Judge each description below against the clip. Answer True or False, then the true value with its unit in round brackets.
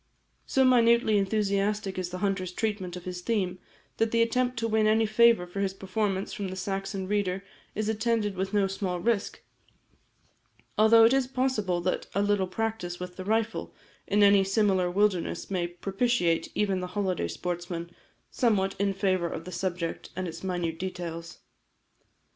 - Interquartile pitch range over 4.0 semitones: False (3.1 semitones)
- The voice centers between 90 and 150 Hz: False (195 Hz)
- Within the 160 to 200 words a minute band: True (165 wpm)